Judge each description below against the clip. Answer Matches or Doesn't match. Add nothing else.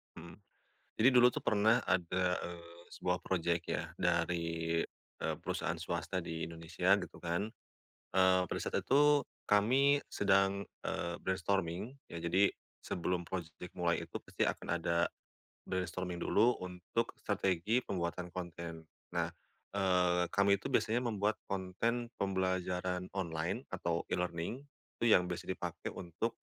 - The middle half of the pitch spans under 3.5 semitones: Matches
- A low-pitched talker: Matches